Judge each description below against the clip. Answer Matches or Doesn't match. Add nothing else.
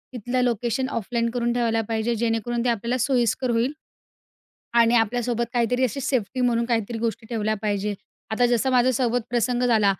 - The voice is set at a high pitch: Matches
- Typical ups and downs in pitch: Doesn't match